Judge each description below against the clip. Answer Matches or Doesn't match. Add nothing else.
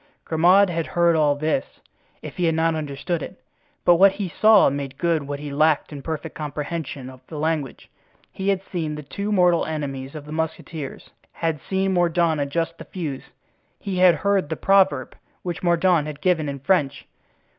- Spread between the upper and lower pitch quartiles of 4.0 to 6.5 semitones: Doesn't match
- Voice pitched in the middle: Matches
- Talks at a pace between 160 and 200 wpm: Matches